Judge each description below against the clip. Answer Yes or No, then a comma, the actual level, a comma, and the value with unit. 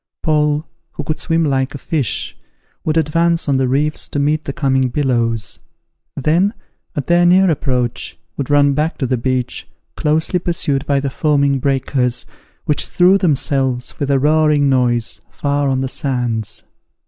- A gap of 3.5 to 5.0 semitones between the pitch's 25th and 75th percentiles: No, average, 3.0 semitones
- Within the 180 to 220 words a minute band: No, average, 160 wpm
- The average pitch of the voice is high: No, medium, 140 Hz